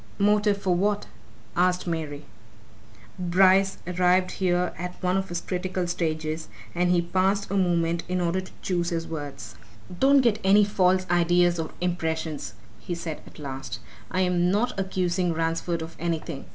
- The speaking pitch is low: No, medium, 180 Hz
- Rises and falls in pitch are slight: Yes, narrow, 2.1 semitones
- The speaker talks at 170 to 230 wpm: No, average, 150 wpm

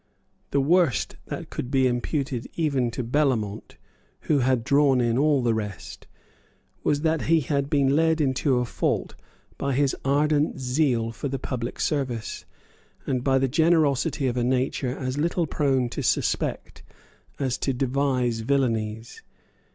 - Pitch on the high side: No, low, 135 Hz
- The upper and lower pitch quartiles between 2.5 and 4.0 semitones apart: Yes, average, 2.9 semitones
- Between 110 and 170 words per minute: Yes, average, 150 wpm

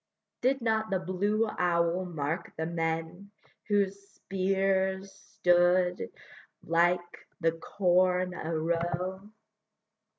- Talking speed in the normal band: No, slow, 95 wpm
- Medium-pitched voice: Yes, medium, 180 Hz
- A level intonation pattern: Yes, narrow, 2.3 semitones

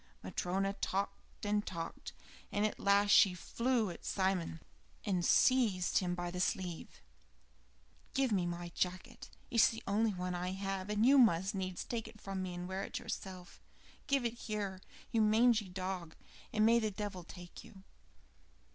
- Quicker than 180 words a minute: No, average, 165 wpm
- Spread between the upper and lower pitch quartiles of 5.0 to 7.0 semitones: No, average, 2.9 semitones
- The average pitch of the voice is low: No, high, 195 Hz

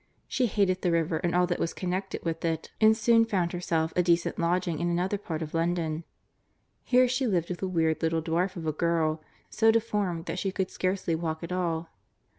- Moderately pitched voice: Yes, medium, 175 Hz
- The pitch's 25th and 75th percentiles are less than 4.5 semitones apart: Yes, narrow, 2.6 semitones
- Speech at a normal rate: No, fast, 210 wpm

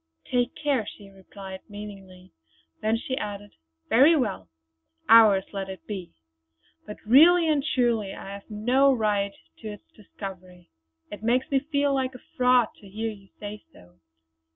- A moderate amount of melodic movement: Yes, average, 4.5 semitones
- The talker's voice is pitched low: No, high, 210 Hz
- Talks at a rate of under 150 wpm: No, average, 155 wpm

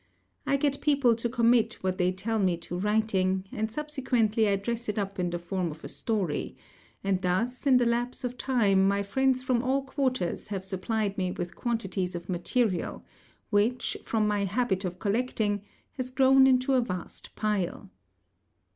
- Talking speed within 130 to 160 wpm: No, average, 175 wpm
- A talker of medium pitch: No, high, 215 Hz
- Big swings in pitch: No, average, 4.7 semitones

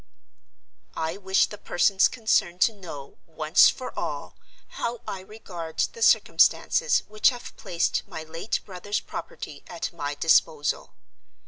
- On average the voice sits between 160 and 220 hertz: Yes, medium, 185 Hz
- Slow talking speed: Yes, slow, 130 wpm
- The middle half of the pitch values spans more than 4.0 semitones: Yes, average, 5.1 semitones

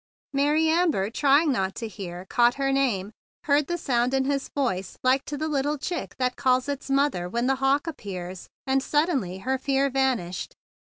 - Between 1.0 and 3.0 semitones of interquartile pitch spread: No, average, 3.9 semitones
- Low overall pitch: No, very high, 270 Hz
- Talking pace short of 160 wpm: No, average, 185 wpm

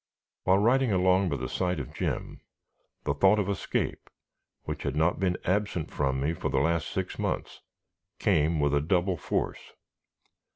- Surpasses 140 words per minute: Yes, average, 160 wpm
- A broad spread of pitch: No, average, 4.6 semitones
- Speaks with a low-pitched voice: Yes, very low, 90 Hz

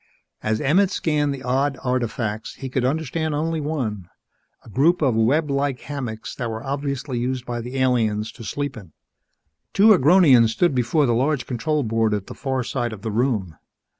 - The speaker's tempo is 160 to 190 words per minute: Yes, average, 180 wpm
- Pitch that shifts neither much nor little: Yes, average, 4.2 semitones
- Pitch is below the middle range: Yes, low, 130 Hz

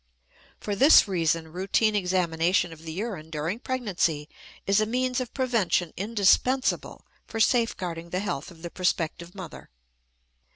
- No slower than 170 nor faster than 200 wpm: No, slow, 135 wpm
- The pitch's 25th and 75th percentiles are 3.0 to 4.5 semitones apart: No, average, 5.0 semitones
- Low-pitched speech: No, medium, 185 Hz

